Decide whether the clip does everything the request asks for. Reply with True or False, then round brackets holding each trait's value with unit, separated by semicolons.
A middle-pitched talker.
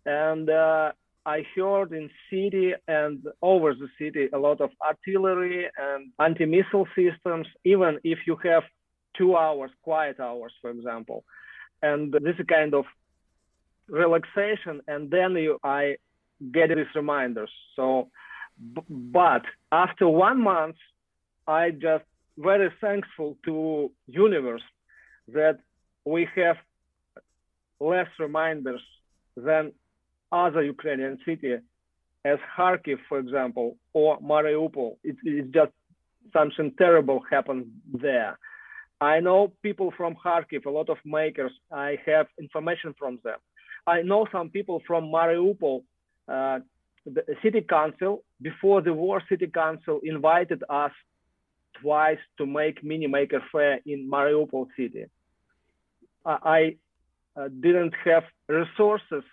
True (155 Hz)